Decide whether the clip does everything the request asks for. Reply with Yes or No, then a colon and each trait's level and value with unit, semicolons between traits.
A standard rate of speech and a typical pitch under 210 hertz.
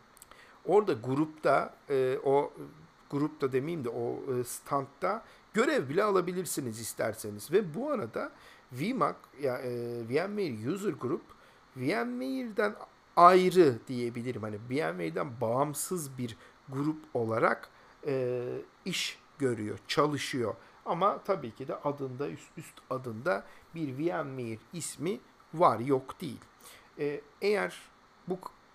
Yes: average, 110 wpm; medium, 140 Hz